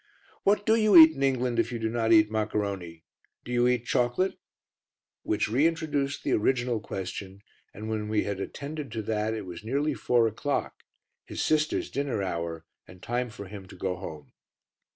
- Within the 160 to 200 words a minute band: Yes, average, 175 wpm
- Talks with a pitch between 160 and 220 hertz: No, low, 115 Hz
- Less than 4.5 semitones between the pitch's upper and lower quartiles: No, average, 5.2 semitones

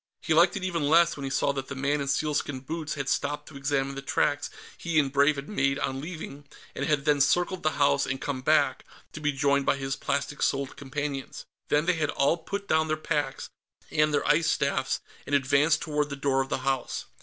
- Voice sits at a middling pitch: Yes, medium, 145 Hz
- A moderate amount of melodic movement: No, narrow, 2.1 semitones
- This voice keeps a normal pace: No, fast, 225 wpm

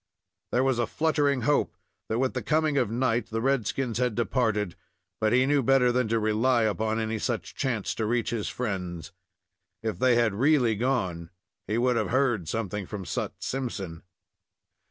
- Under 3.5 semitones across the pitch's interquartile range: Yes, average, 3.1 semitones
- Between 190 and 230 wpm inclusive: No, average, 175 wpm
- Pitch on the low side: Yes, low, 115 Hz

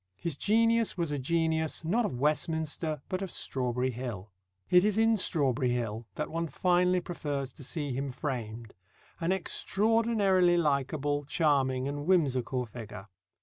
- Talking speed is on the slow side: No, average, 145 wpm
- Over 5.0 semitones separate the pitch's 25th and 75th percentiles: Yes, wide, 5.6 semitones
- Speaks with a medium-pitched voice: Yes, medium, 150 Hz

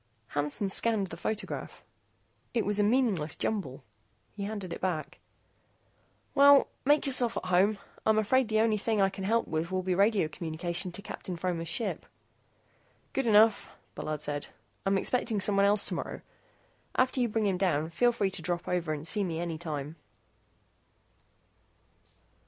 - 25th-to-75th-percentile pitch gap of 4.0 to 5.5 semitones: Yes, average, 4.5 semitones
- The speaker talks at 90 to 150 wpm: No, average, 160 wpm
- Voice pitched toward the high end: Yes, high, 195 Hz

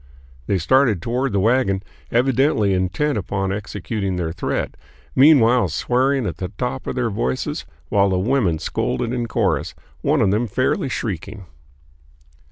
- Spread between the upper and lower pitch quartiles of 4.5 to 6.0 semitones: Yes, average, 4.9 semitones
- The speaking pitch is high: No, low, 110 Hz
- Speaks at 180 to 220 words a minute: No, average, 145 wpm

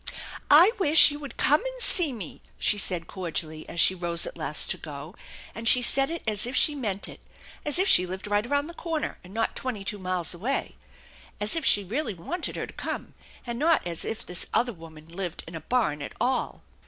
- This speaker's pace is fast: Yes, fast, 225 wpm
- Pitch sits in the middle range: No, high, 210 Hz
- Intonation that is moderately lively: No, wide, 8.4 semitones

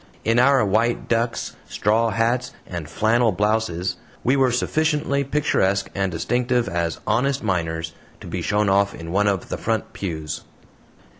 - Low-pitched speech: Yes, low, 110 Hz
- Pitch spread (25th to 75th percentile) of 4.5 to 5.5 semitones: Yes, average, 4.9 semitones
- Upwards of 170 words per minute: No, average, 150 wpm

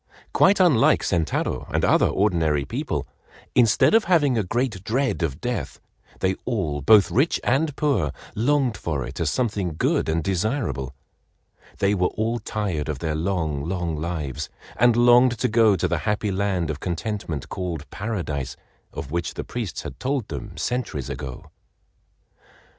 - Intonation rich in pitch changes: Yes, wide, 7.1 semitones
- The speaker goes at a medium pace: Yes, average, 155 wpm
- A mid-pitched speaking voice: No, very low, 95 Hz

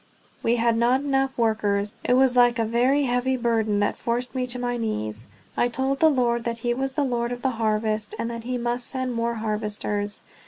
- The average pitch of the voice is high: Yes, high, 240 Hz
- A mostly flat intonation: Yes, narrow, 2.2 semitones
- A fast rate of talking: Yes, fast, 210 wpm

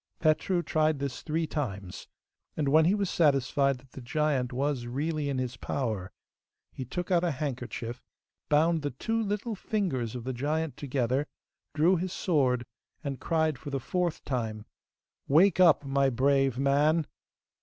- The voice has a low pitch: No, medium, 145 Hz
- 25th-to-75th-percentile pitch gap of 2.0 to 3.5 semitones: No, average, 3.9 semitones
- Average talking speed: Yes, average, 155 wpm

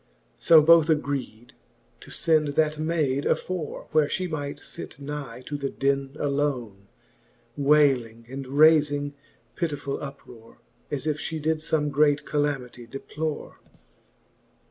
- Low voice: No, medium, 145 Hz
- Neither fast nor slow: No, slow, 120 wpm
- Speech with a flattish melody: Yes, narrow, 2.1 semitones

